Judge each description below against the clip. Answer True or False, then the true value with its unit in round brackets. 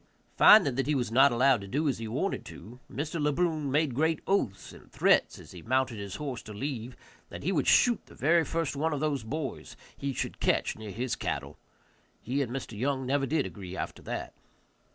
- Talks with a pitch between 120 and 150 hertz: True (135 Hz)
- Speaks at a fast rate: True (215 wpm)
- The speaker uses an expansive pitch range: False (4.3 semitones)